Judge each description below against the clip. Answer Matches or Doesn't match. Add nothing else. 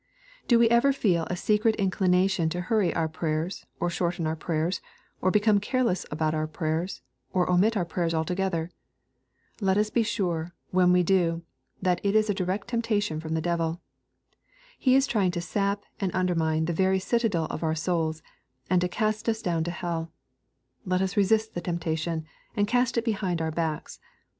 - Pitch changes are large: Doesn't match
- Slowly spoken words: Doesn't match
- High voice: Doesn't match